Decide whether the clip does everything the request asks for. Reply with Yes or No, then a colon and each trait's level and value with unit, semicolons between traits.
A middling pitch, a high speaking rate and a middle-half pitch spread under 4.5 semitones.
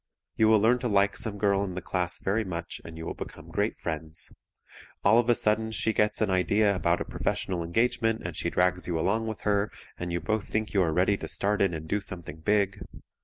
No: low, 100 Hz; fast, 230 wpm; average, 3.6 semitones